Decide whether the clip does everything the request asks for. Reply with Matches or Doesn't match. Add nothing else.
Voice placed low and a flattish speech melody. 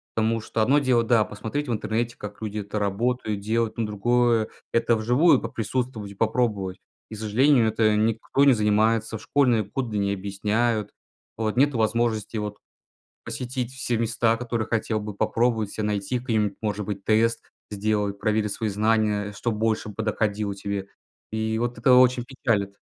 Matches